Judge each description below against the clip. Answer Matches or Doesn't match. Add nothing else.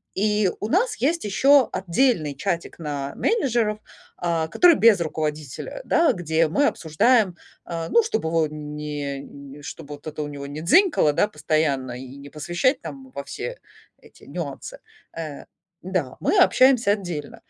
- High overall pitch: Doesn't match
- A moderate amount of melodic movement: Doesn't match